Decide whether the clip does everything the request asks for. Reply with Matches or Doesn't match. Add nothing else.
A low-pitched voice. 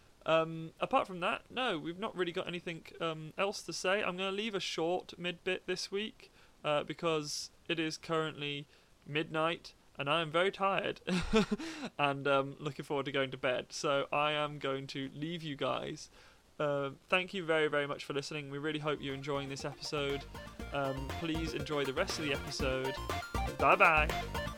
Doesn't match